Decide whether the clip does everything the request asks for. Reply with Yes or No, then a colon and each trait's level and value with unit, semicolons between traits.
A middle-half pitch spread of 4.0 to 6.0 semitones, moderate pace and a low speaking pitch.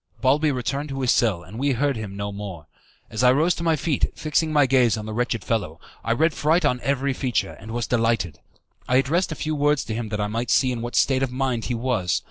No: average, 4.3 semitones; fast, 250 wpm; low, 125 Hz